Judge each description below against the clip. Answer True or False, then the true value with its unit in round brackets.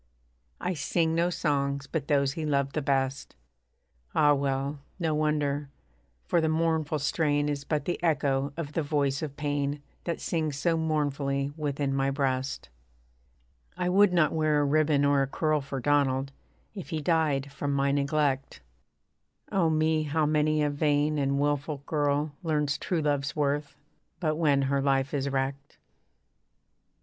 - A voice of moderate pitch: True (145 Hz)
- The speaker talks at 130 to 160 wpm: True (155 wpm)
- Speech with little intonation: True (1.9 semitones)